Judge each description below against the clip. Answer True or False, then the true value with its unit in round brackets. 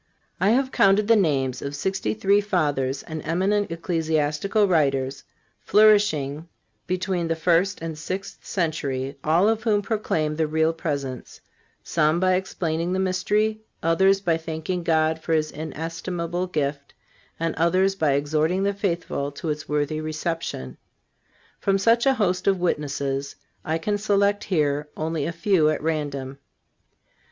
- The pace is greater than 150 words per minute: False (140 wpm)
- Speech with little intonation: False (4.2 semitones)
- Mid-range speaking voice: True (165 Hz)